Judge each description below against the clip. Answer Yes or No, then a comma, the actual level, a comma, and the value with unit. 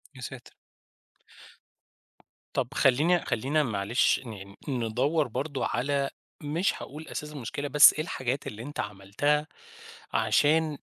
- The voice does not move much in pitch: No, average, 4.1 semitones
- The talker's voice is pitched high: No, medium, 140 Hz